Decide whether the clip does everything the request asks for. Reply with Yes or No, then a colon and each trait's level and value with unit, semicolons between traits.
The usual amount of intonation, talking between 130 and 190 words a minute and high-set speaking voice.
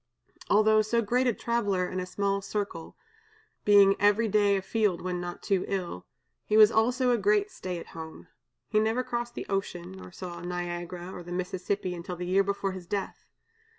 Yes: average, 3.3 semitones; average, 185 wpm; high, 195 Hz